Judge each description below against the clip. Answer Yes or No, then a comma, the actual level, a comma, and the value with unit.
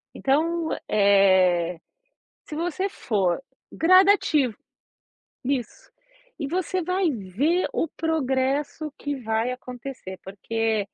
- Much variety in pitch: Yes, wide, 7.4 semitones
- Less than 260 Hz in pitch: No, very high, 265 Hz